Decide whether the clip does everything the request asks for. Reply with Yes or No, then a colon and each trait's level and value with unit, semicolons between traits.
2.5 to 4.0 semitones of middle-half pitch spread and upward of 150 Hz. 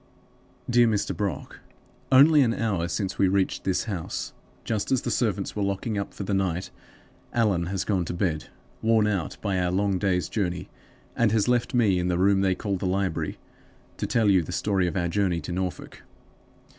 No: average, 2.8 semitones; very low, 95 Hz